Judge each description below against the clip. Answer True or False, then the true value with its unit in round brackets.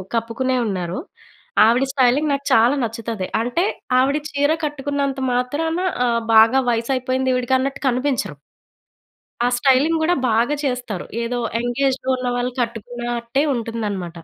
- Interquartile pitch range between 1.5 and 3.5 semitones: True (2.8 semitones)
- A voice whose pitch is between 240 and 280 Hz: True (245 Hz)